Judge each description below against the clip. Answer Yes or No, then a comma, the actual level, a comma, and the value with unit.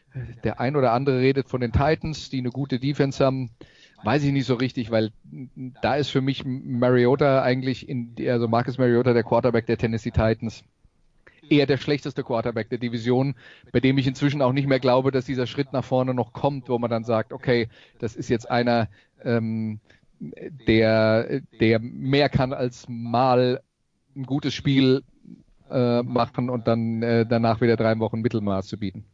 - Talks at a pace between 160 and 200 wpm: Yes, average, 180 wpm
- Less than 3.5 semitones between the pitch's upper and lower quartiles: Yes, narrow, 2.5 semitones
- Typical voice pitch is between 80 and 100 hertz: No, low, 125 Hz